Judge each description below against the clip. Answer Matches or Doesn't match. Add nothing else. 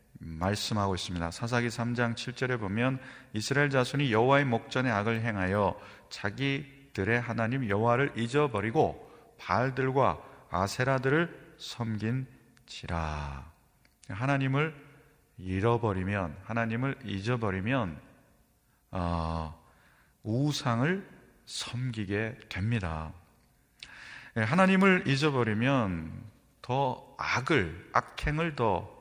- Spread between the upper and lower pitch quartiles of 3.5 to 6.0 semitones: Matches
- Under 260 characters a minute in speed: Matches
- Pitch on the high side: Doesn't match